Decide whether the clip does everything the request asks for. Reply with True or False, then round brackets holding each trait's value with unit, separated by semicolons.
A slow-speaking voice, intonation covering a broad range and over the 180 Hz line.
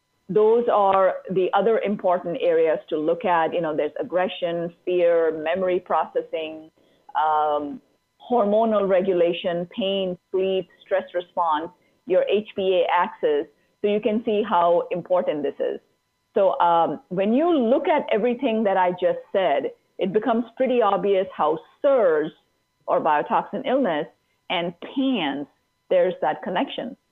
True (130 wpm; 5.7 semitones; 190 Hz)